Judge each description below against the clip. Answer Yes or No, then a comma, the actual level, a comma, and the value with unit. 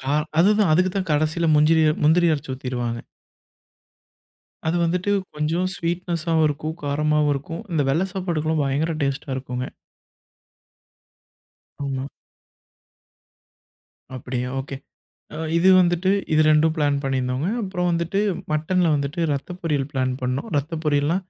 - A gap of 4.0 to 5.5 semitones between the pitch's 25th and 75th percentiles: No, average, 3.6 semitones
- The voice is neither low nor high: Yes, medium, 155 Hz